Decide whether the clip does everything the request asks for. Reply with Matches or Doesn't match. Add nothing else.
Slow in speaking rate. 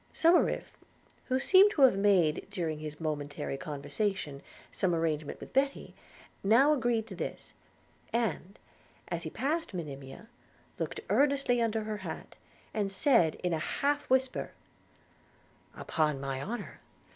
Matches